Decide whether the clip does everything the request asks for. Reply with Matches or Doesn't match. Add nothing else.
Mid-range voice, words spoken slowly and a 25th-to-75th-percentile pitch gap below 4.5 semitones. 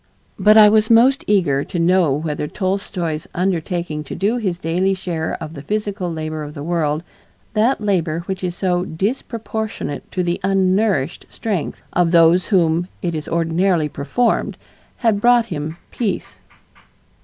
Doesn't match